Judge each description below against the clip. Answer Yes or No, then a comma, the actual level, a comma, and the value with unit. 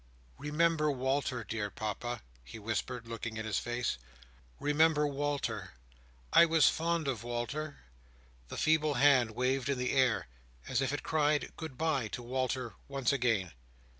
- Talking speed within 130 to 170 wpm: Yes, average, 145 wpm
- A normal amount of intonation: Yes, average, 3.9 semitones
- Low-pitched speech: Yes, low, 130 Hz